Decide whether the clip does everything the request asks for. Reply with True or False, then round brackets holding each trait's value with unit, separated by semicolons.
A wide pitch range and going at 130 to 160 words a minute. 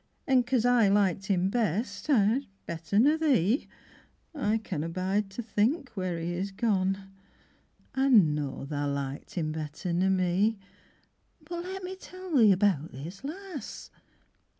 True (6.3 semitones; 145 wpm)